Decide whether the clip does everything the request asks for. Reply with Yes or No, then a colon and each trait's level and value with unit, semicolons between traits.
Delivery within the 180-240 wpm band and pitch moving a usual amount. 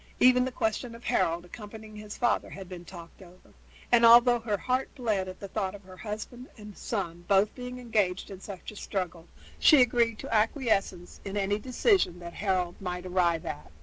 Yes: average, 185 wpm; average, 4.3 semitones